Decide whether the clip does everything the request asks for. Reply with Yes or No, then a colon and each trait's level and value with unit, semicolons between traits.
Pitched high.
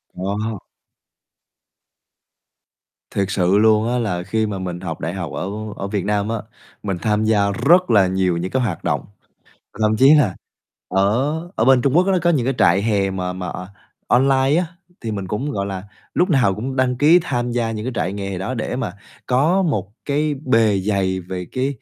No: low, 110 Hz